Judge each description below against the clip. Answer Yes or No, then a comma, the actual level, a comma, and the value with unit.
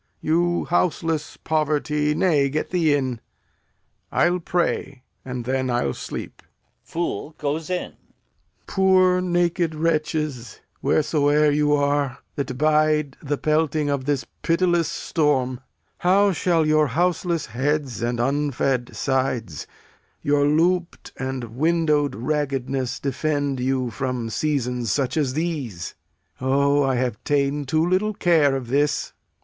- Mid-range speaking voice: Yes, medium, 145 Hz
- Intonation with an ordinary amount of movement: Yes, average, 3.4 semitones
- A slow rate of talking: Yes, slow, 120 wpm